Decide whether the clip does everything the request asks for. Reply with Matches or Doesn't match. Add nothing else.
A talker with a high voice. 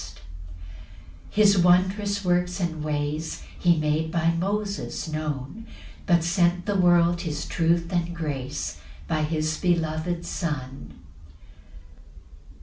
Doesn't match